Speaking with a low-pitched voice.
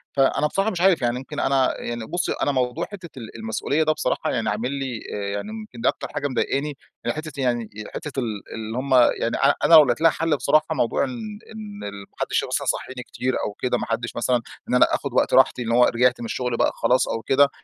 Yes: low, 130 Hz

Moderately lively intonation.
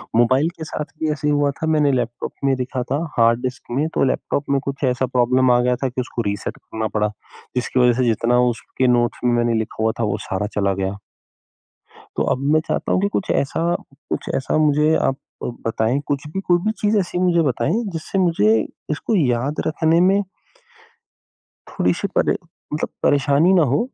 Yes: average, 4.6 semitones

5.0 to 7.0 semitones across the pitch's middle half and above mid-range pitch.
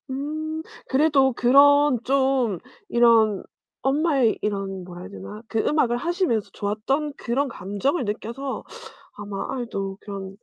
Yes: wide, 5.4 semitones; high, 245 Hz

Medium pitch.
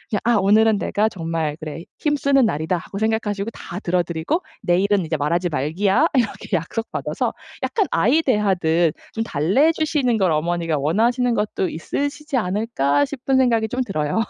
No: high, 200 Hz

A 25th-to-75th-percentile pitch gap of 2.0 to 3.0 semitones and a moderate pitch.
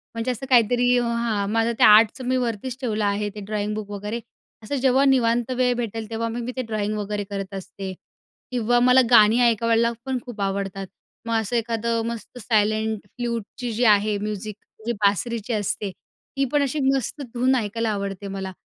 No: average, 2.7 semitones; high, 225 Hz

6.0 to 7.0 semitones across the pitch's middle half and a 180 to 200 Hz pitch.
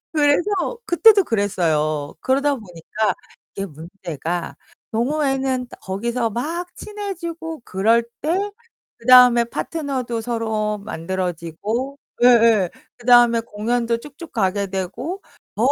No: wide, 6.4 semitones; high, 235 Hz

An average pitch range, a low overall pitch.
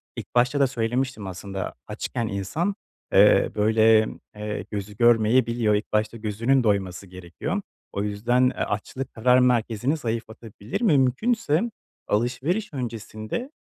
Yes: average, 3.7 semitones; low, 115 Hz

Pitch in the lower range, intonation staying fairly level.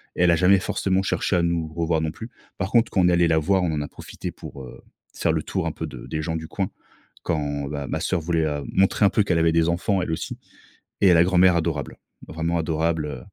Yes: very low, 85 Hz; narrow, 2.3 semitones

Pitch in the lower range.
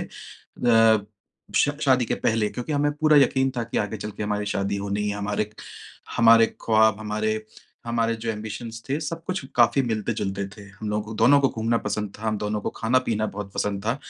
Yes: low, 110 Hz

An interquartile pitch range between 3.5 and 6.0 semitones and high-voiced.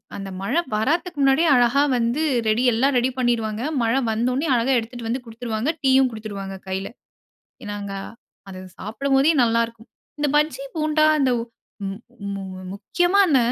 Yes: average, 4.0 semitones; high, 240 Hz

